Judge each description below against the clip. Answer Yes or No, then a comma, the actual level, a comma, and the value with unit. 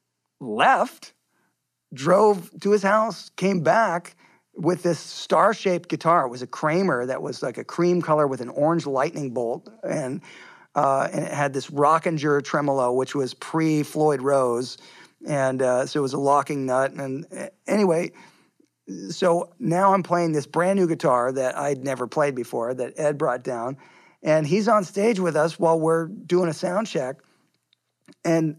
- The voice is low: No, medium, 155 Hz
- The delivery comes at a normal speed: Yes, average, 165 wpm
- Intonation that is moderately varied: Yes, average, 4.6 semitones